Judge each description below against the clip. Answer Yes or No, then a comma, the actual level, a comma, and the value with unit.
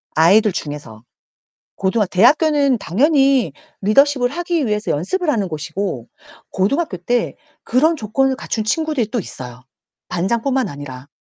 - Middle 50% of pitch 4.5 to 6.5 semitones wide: No, wide, 7.8 semitones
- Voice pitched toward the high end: Yes, high, 220 Hz